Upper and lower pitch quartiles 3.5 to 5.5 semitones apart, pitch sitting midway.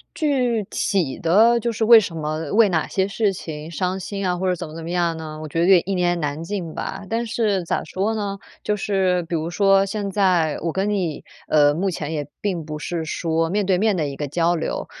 Yes: average, 3.8 semitones; medium, 180 Hz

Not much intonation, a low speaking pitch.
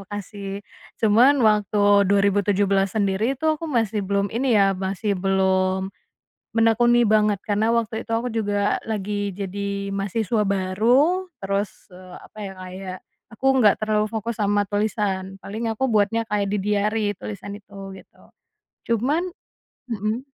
No: narrow, 2.2 semitones; high, 205 Hz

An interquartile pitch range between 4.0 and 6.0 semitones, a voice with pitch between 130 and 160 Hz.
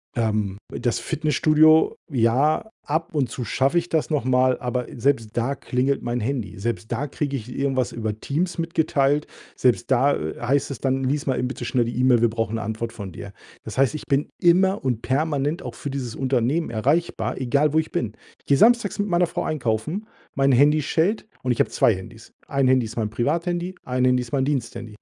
Yes: average, 4.3 semitones; low, 135 Hz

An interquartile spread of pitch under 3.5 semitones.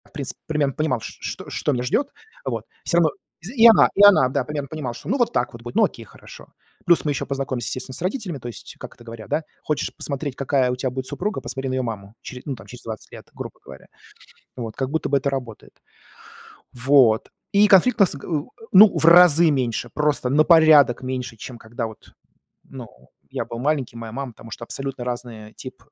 No: average, 4.3 semitones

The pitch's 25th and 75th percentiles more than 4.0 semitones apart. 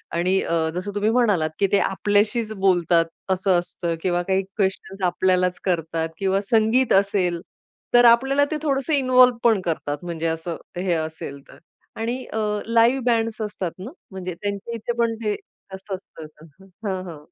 Yes: average, 4.4 semitones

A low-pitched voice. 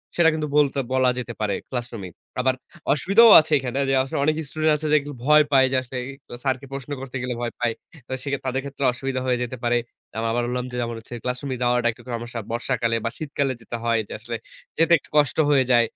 Yes: low, 130 Hz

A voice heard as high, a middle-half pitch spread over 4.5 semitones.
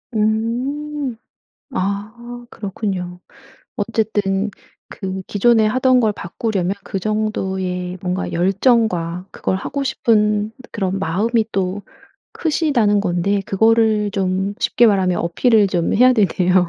No: high, 205 Hz; average, 3.3 semitones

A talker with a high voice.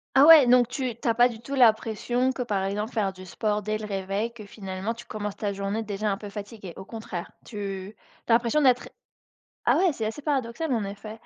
Yes: high, 220 Hz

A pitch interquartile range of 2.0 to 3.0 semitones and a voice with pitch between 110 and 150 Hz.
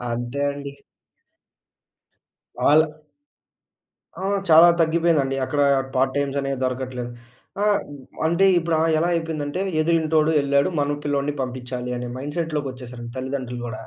No: average, 3.7 semitones; medium, 140 Hz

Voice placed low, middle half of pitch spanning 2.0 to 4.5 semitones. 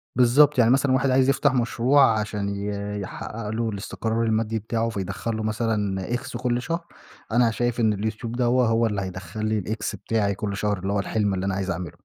Yes: low, 110 Hz; average, 3.0 semitones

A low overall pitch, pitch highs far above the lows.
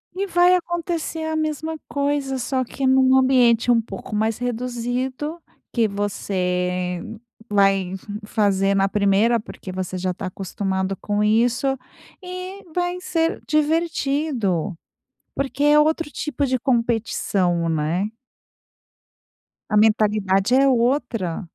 No: high, 235 Hz; wide, 6.8 semitones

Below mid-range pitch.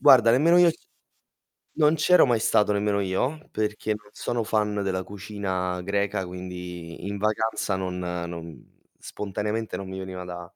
Yes: low, 100 Hz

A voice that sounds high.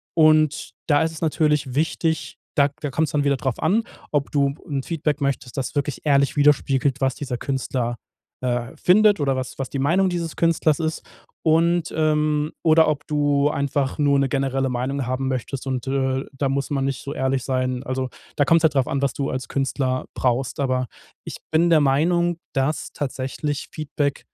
No: medium, 140 Hz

